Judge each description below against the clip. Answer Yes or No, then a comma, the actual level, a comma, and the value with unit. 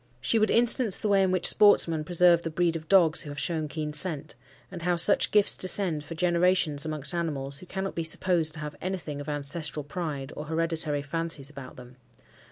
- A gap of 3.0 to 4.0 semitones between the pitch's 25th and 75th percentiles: Yes, average, 3.3 semitones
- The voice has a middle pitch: Yes, medium, 165 Hz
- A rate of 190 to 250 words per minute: Yes, average, 200 wpm